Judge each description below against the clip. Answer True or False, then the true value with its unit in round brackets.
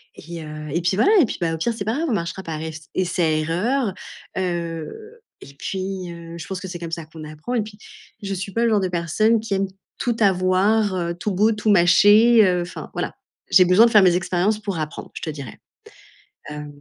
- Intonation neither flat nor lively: True (4.1 semitones)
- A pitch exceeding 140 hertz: True (185 Hz)